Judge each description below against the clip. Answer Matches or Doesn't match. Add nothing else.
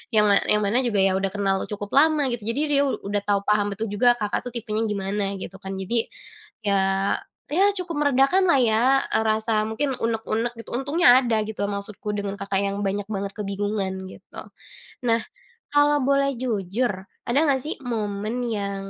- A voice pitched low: Doesn't match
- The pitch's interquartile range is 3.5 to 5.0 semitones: Matches